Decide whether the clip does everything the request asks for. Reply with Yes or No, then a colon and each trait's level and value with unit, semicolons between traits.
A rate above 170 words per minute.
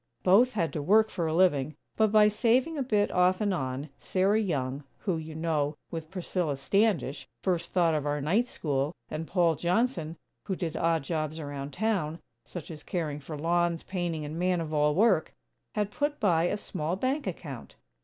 Yes: average, 185 wpm